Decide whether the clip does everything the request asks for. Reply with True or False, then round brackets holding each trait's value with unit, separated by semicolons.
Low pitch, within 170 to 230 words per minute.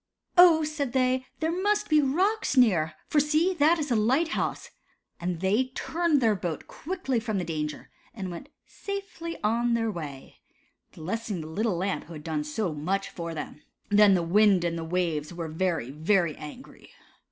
False (210 Hz; 175 wpm)